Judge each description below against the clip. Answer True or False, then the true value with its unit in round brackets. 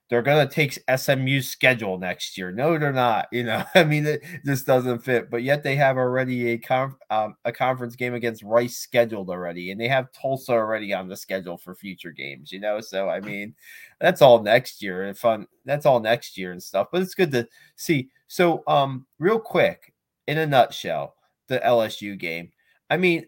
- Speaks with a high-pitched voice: False (120 Hz)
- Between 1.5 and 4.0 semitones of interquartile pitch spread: False (5.3 semitones)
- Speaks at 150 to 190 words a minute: False (205 wpm)